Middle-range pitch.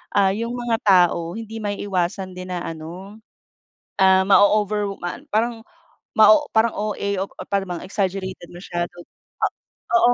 No: high, 200 Hz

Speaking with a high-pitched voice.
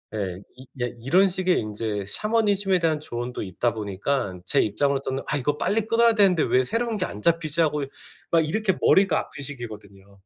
No: medium, 145 Hz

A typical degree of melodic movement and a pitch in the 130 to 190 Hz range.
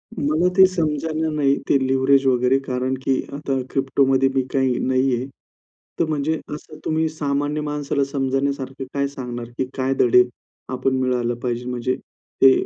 No: narrow, 2.3 semitones; low, 135 Hz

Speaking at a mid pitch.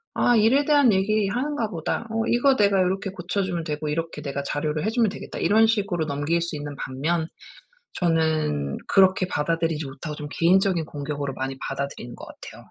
Yes: medium, 170 Hz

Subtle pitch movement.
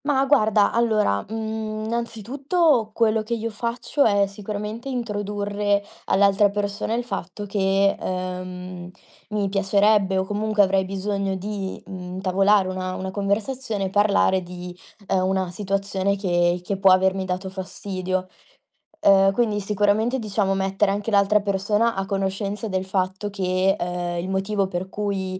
Yes: narrow, 2.0 semitones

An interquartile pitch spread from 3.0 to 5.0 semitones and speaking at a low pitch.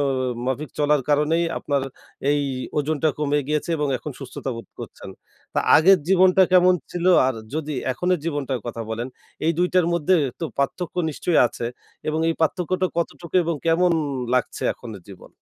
No: average, 3.9 semitones; medium, 155 Hz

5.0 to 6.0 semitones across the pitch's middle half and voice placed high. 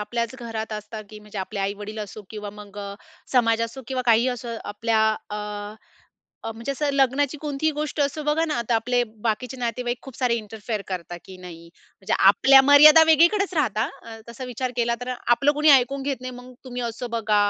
No: average, 3.9 semitones; high, 235 Hz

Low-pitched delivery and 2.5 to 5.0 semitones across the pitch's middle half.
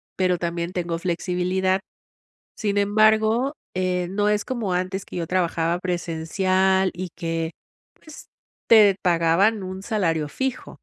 No: medium, 185 Hz; average, 2.9 semitones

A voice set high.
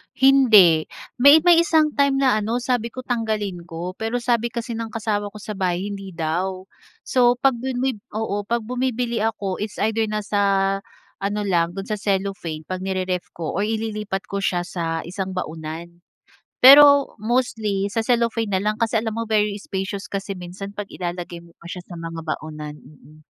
Yes: high, 205 Hz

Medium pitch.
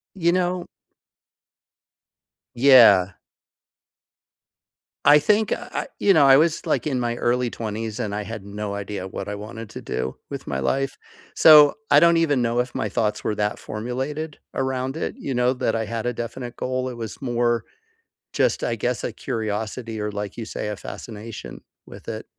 No: low, 120 Hz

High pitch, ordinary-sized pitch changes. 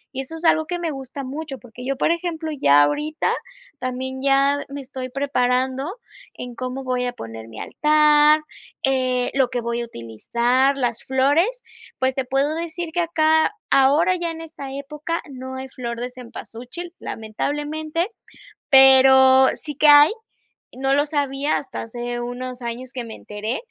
Yes: very high, 270 Hz; average, 3.2 semitones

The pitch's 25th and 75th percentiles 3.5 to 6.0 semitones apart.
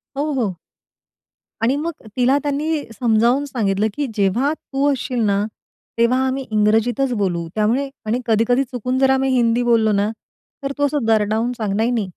Yes: average, 3.8 semitones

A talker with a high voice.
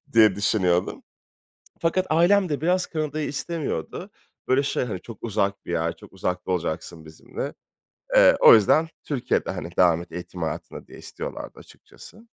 No: low, 110 Hz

